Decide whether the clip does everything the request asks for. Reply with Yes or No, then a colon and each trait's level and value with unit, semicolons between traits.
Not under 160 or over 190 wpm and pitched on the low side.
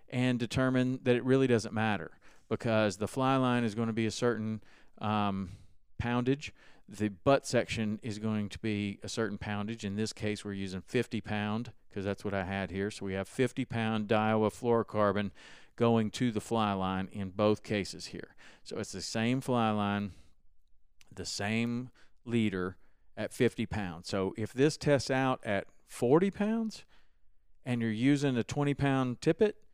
Yes: average, 170 wpm; low, 110 Hz